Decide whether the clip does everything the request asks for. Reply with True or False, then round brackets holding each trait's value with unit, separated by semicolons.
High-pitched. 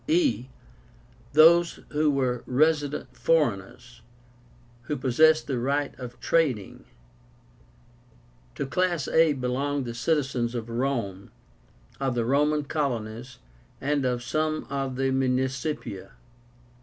False (135 Hz)